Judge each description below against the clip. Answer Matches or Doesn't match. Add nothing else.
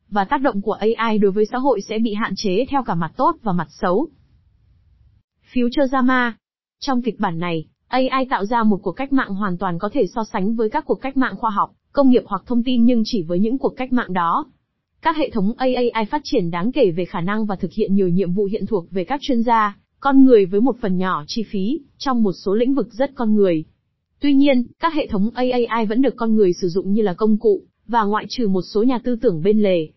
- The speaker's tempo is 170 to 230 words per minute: Doesn't match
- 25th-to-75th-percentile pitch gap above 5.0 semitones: Doesn't match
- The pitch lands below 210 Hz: Doesn't match